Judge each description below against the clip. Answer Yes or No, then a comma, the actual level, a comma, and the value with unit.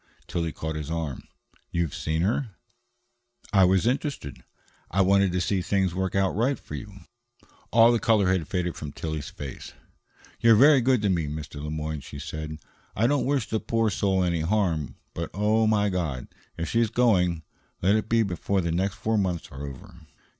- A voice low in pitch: Yes, very low, 95 Hz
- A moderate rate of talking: Yes, average, 185 wpm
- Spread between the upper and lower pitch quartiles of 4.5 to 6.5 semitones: Yes, average, 5.2 semitones